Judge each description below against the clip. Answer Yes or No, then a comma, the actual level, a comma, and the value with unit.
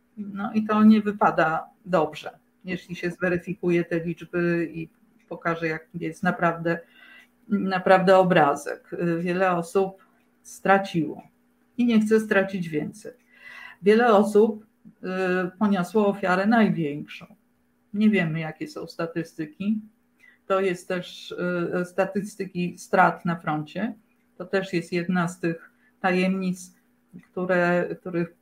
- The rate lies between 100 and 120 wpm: Yes, slow, 110 wpm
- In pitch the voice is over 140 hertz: Yes, medium, 185 Hz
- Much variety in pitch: No, average, 3.4 semitones